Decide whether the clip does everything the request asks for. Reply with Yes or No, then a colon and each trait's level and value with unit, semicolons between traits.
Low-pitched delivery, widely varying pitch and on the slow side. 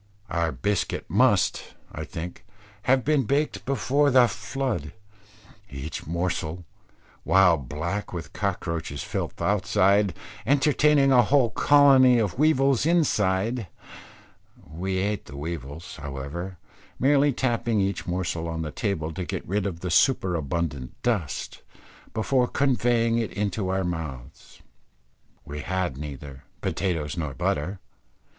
Yes: very low, 95 Hz; wide, 7.1 semitones; slow, 120 wpm